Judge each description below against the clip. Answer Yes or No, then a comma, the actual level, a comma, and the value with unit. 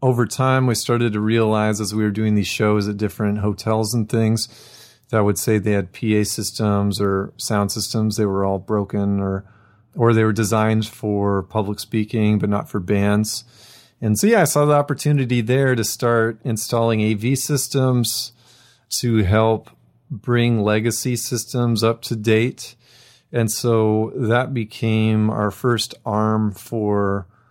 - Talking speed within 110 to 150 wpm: No, average, 160 wpm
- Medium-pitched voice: No, low, 110 Hz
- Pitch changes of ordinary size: No, narrow, 2.3 semitones